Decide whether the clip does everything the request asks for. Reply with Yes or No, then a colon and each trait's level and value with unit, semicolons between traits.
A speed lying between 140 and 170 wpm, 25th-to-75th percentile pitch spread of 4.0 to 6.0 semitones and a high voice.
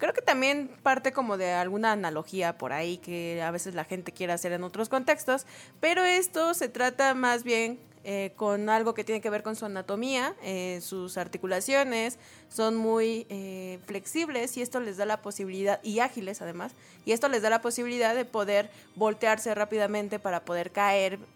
No: average, 185 wpm; average, 4.3 semitones; high, 215 Hz